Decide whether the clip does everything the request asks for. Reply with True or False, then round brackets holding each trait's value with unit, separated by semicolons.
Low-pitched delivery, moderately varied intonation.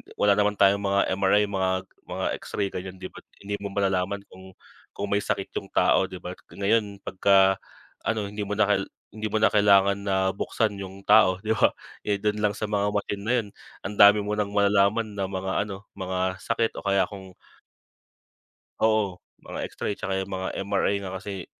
False (100 Hz; 1.2 semitones)